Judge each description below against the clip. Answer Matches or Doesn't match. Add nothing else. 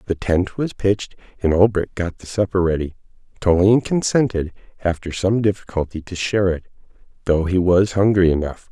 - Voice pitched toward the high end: Doesn't match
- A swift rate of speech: Doesn't match